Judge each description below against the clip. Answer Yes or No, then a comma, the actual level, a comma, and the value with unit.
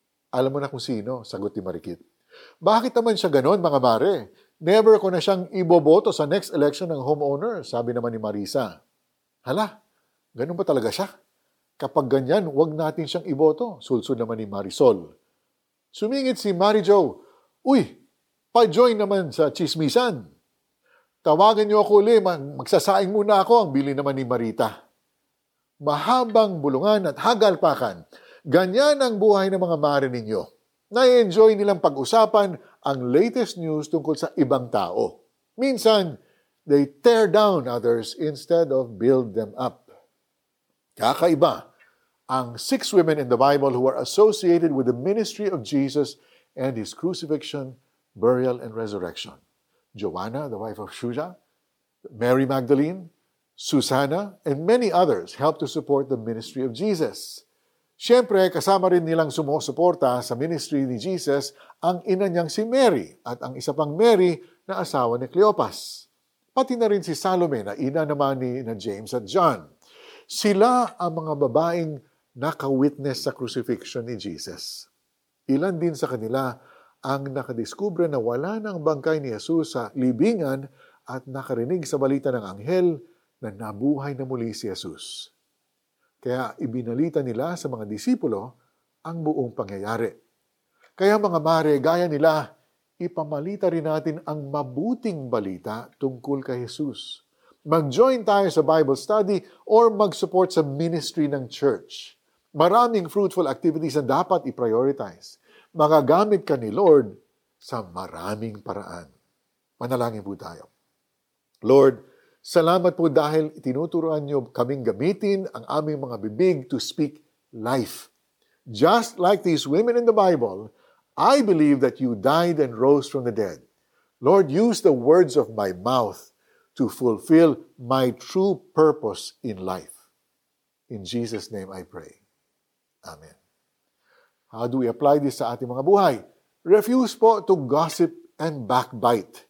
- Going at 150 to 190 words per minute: No, average, 140 wpm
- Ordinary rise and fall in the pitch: No, wide, 7.0 semitones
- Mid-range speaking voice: Yes, medium, 155 Hz